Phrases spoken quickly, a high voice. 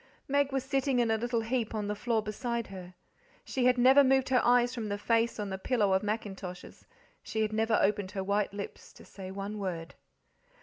Yes: fast, 210 wpm; high, 220 Hz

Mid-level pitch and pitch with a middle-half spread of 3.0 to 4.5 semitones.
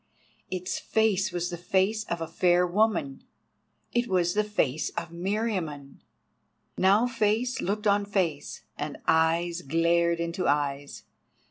Yes: medium, 180 Hz; average, 3.9 semitones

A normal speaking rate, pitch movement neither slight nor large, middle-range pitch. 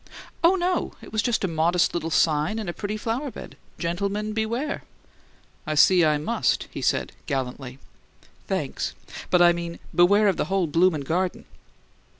Yes: average, 160 wpm; average, 4.8 semitones; medium, 180 Hz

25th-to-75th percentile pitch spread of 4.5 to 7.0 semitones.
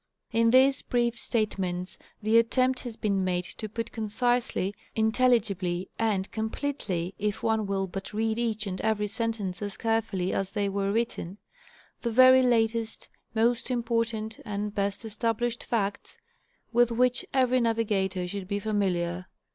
No: average, 2.9 semitones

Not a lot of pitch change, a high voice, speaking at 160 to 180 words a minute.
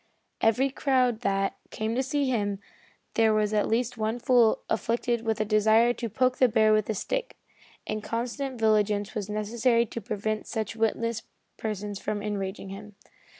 Yes: narrow, 2.1 semitones; high, 220 Hz; average, 170 wpm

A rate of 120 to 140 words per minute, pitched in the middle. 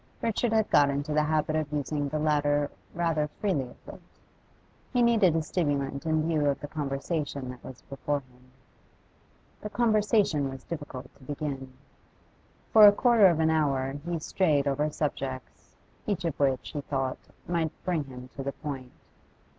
No: average, 165 wpm; medium, 150 Hz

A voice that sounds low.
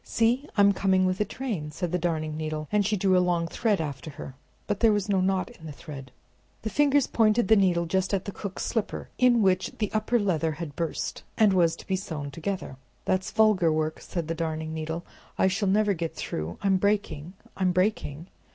No: medium, 185 Hz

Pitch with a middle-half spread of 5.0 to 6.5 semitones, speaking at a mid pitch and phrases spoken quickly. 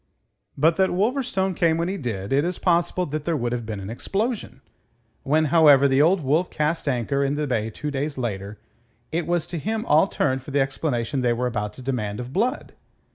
Yes: wide, 5.5 semitones; medium, 145 Hz; fast, 210 wpm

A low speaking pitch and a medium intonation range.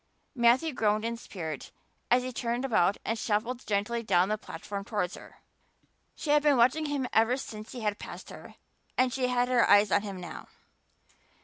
No: high, 230 Hz; average, 3.5 semitones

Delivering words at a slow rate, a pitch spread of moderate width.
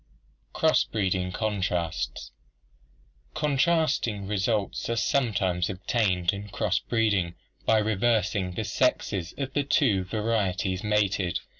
Yes: slow, 115 wpm; average, 3.5 semitones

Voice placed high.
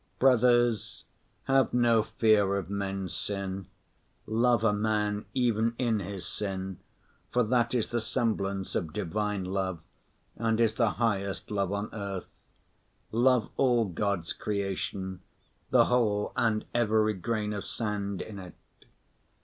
No: low, 105 Hz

